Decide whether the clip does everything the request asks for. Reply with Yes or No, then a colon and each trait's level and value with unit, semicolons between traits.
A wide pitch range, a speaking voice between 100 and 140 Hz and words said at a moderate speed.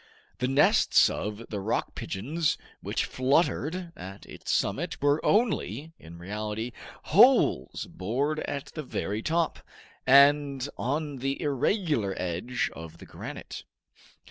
No: wide, 6.1 semitones; low, 135 Hz; slow, 120 wpm